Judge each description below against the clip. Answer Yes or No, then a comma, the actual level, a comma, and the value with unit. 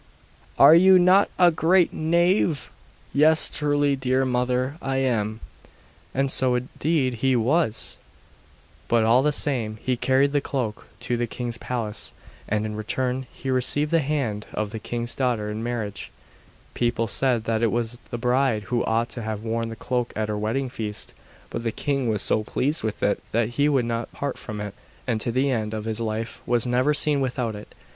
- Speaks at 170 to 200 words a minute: Yes, average, 185 wpm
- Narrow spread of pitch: No, average, 3.6 semitones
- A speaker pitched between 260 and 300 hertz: No, low, 125 Hz